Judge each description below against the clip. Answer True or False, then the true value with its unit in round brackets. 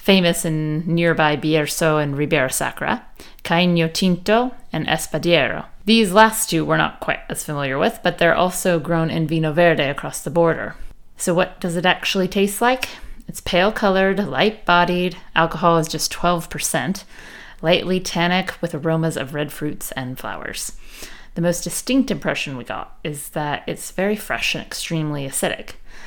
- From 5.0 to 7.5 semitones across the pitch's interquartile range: False (3.0 semitones)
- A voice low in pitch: False (170 Hz)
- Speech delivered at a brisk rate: False (160 wpm)